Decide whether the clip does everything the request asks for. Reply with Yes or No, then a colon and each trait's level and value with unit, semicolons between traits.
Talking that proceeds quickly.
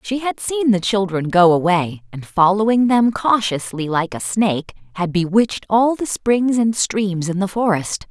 No: average, 180 wpm